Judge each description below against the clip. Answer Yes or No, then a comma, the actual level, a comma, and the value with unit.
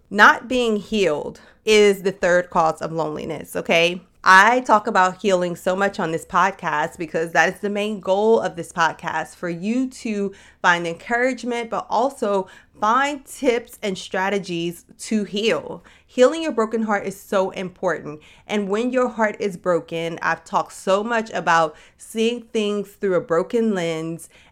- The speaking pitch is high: Yes, high, 195 Hz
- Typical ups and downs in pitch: Yes, average, 4.2 semitones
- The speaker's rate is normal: Yes, average, 160 wpm